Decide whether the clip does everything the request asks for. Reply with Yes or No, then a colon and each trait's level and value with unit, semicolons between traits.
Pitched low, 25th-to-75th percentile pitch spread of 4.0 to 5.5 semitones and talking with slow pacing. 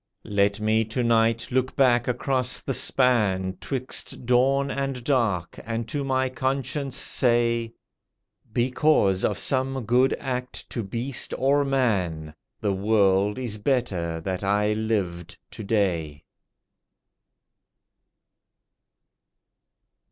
Yes: low, 115 Hz; average, 4.3 semitones; slow, 105 wpm